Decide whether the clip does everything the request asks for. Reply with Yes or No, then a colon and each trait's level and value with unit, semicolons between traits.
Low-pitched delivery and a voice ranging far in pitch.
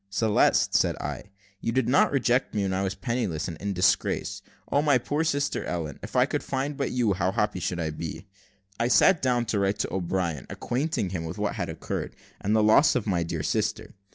Yes: low, 105 Hz; wide, 5.7 semitones